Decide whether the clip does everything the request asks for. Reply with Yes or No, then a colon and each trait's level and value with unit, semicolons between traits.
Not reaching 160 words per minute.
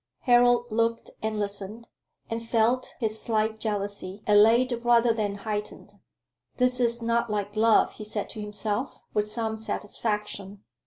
Yes: average, 140 wpm